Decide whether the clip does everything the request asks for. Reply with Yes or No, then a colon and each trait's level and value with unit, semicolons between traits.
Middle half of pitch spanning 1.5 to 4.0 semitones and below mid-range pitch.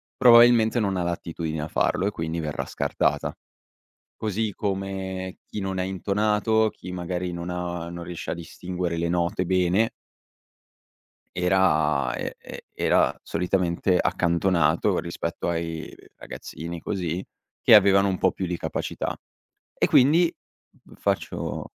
Yes: narrow, 2.4 semitones; very low, 90 Hz